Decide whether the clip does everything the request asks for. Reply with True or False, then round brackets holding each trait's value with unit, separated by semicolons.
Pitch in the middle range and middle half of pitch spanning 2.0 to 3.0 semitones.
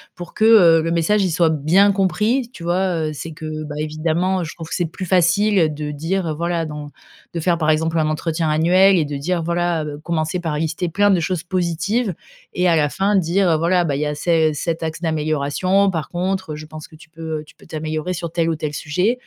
True (165 Hz; 2.7 semitones)